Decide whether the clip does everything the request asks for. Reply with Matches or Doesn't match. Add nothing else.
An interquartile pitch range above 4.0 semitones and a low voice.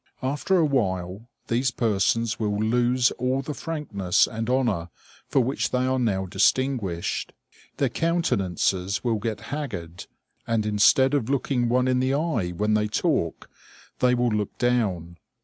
Matches